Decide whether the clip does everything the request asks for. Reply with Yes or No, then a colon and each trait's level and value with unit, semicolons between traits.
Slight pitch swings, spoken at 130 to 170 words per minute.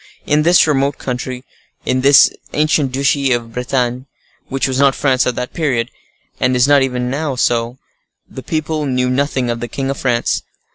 No: narrow, 2.2 semitones; average, 180 wpm